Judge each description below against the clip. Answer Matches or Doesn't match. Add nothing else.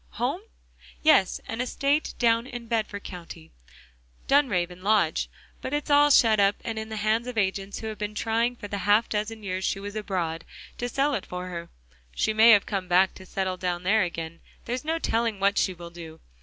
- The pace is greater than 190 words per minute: Matches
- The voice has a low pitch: Doesn't match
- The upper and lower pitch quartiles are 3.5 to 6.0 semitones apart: Matches